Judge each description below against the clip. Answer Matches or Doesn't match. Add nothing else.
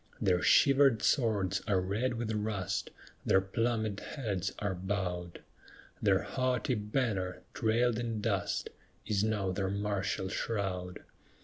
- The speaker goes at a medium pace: Doesn't match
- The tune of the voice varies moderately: Matches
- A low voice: Matches